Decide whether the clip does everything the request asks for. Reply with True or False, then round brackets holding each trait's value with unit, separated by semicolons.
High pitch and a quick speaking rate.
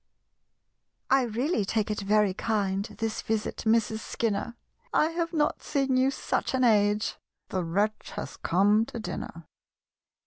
False (220 Hz; 140 wpm)